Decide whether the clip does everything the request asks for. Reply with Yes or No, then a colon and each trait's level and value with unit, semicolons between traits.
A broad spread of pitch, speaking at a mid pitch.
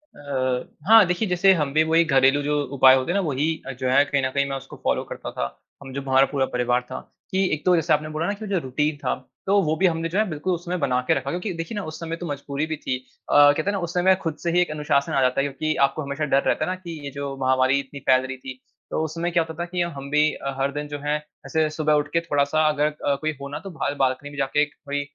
No: average, 3.3 semitones; medium, 150 Hz